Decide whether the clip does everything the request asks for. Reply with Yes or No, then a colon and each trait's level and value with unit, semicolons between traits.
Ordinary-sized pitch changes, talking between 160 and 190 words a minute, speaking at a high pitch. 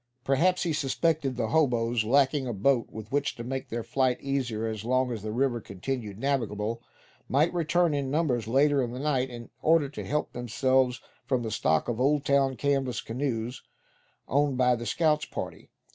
No: average, 3.2 semitones; average, 180 wpm; low, 130 Hz